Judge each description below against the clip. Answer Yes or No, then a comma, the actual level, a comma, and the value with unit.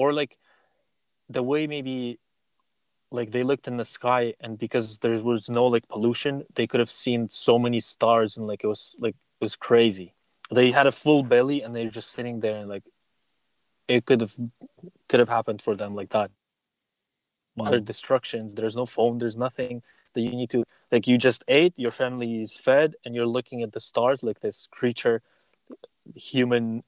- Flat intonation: Yes, narrow, 2.0 semitones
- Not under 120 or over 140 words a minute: No, average, 190 wpm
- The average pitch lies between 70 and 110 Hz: No, low, 120 Hz